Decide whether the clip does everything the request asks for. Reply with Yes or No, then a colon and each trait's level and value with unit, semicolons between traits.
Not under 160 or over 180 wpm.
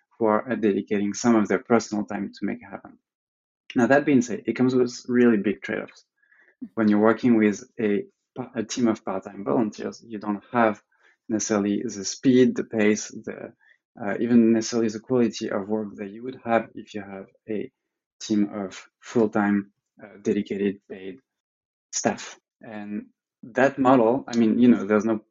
Yes: average, 170 wpm